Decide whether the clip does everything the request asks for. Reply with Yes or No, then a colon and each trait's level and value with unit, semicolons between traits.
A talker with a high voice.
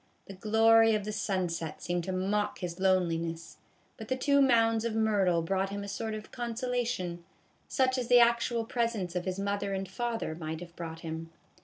Yes: high, 200 Hz